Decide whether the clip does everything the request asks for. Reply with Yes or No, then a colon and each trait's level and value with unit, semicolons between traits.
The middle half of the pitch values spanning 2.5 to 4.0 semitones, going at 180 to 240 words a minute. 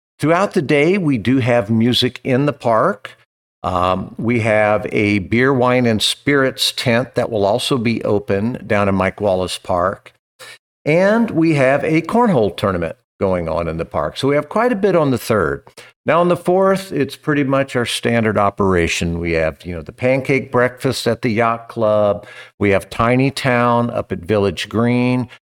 No: average, 4.8 semitones; average, 185 wpm